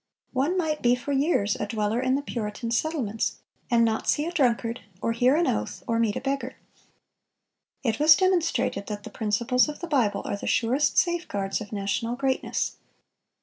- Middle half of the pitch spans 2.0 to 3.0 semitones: No, average, 4.7 semitones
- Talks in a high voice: Yes, high, 245 Hz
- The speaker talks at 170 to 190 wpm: Yes, average, 180 wpm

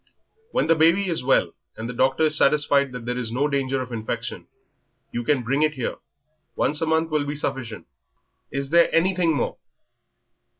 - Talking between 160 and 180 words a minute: Yes, average, 175 wpm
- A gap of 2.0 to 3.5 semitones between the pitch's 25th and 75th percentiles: No, average, 4.0 semitones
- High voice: No, medium, 140 Hz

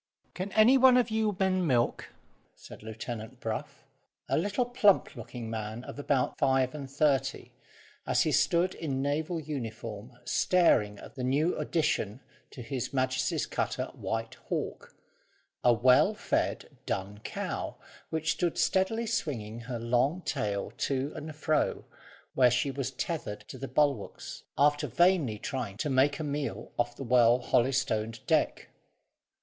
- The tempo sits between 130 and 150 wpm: Yes, average, 145 wpm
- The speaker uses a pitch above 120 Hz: Yes, low, 135 Hz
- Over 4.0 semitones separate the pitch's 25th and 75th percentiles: Yes, average, 5.1 semitones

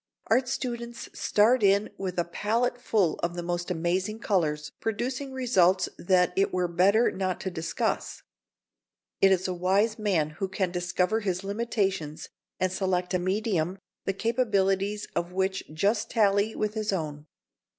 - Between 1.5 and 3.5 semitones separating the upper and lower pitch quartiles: Yes, average, 3.2 semitones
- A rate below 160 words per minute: Yes, average, 150 wpm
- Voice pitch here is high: Yes, high, 195 Hz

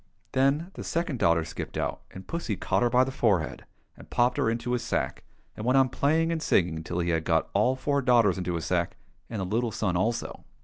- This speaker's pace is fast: Yes, fast, 225 wpm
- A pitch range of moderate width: No, wide, 6.5 semitones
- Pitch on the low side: Yes, low, 115 Hz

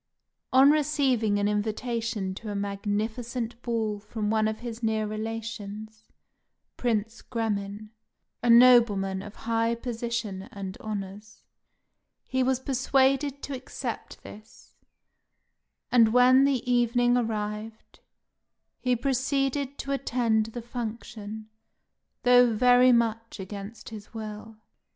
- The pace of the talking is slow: Yes, slow, 110 wpm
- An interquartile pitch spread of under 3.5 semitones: Yes, average, 2.7 semitones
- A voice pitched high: Yes, high, 225 Hz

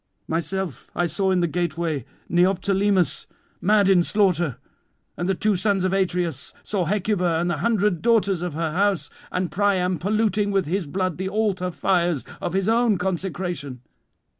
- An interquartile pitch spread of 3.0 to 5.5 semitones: No, narrow, 2.6 semitones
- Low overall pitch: No, medium, 185 Hz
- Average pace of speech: Yes, average, 160 wpm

